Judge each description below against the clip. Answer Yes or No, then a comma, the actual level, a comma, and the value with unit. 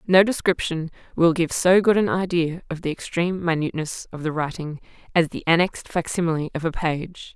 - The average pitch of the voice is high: No, medium, 165 Hz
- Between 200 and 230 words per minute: No, average, 180 wpm